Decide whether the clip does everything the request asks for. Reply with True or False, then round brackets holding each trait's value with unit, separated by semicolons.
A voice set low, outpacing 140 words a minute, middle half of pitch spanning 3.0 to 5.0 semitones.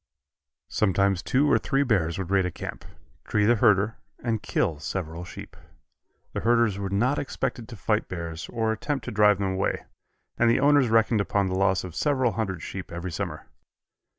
True (105 Hz; 180 wpm; 3.8 semitones)